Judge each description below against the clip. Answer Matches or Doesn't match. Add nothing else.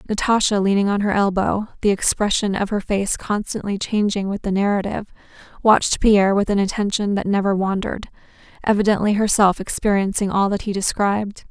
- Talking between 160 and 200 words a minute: Doesn't match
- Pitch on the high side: Matches